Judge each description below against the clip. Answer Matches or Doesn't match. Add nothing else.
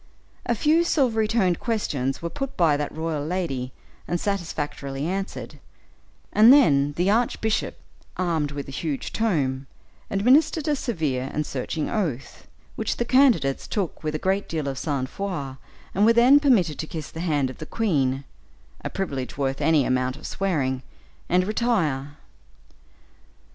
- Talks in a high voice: Doesn't match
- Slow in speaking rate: Doesn't match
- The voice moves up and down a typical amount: Doesn't match